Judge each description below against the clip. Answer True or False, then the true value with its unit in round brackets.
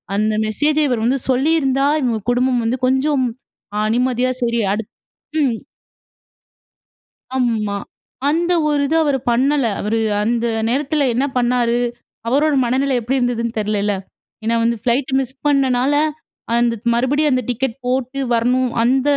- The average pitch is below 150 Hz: False (255 Hz)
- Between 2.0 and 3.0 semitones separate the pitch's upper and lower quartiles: True (2.6 semitones)